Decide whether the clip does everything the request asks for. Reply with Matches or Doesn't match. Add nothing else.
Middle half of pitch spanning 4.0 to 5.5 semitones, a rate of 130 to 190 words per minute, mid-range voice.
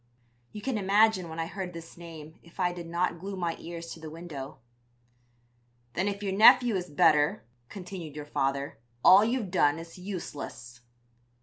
Doesn't match